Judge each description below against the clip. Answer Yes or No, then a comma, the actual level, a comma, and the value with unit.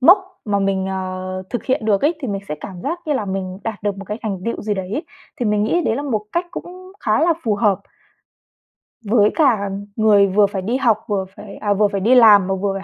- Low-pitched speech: No, high, 210 Hz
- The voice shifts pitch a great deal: No, average, 4.3 semitones